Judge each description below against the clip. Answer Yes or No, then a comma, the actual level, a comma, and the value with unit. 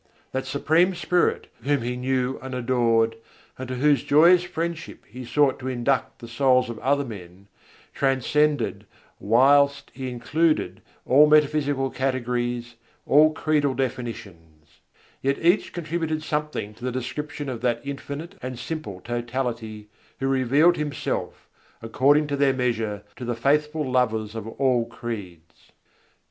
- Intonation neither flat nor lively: Yes, average, 3.7 semitones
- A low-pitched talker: Yes, low, 130 Hz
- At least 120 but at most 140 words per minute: Yes, slow, 135 wpm